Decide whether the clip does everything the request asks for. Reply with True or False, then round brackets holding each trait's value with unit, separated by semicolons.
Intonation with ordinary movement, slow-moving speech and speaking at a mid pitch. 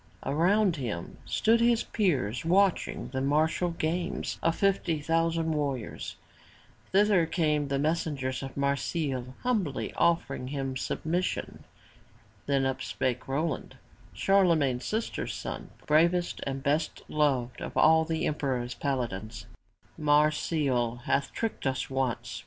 True (4.1 semitones; 120 wpm; 150 Hz)